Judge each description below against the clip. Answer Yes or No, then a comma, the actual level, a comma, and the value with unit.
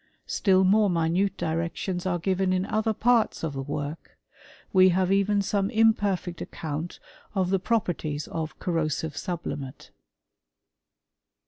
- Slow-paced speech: Yes, slow, 120 wpm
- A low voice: No, medium, 185 Hz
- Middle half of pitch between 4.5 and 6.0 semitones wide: No, average, 3.3 semitones